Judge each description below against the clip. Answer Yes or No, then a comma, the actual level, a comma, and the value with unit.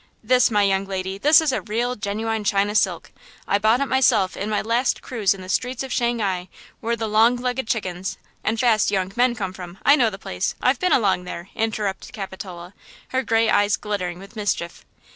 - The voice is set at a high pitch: Yes, high, 215 Hz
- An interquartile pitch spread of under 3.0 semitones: No, average, 3.8 semitones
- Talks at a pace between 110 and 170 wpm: No, average, 200 wpm